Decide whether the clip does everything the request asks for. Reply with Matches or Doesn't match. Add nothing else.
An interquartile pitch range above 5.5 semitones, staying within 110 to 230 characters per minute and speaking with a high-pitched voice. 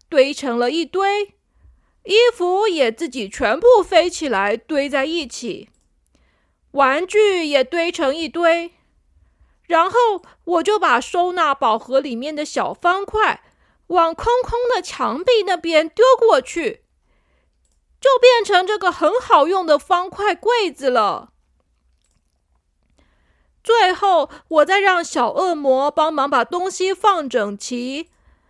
Matches